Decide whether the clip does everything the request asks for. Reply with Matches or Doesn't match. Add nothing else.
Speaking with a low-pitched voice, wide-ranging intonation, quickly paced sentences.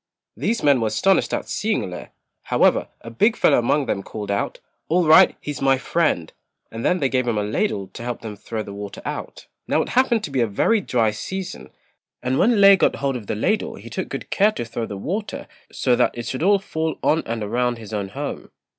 Matches